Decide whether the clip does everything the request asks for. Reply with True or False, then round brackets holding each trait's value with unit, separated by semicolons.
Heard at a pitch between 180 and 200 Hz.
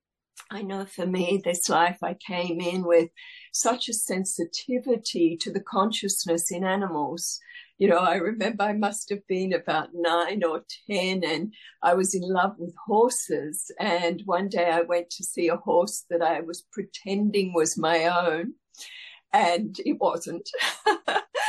True (185 Hz)